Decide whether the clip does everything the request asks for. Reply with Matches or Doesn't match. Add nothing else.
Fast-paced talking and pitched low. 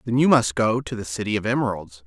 Matches